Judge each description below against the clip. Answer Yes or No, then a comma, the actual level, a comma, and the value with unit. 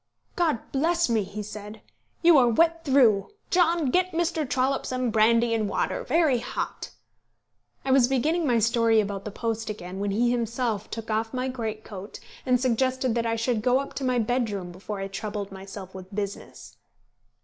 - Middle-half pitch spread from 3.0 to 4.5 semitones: Yes, average, 3.8 semitones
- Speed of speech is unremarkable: Yes, average, 175 wpm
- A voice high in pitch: Yes, high, 230 Hz